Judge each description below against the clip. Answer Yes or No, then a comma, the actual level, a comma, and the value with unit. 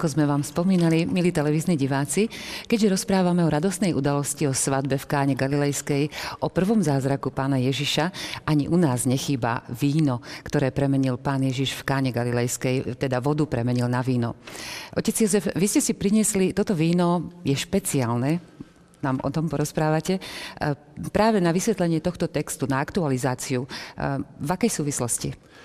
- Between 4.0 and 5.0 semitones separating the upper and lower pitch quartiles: Yes, average, 4.4 semitones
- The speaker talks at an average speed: Yes, average, 145 wpm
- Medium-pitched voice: Yes, medium, 145 Hz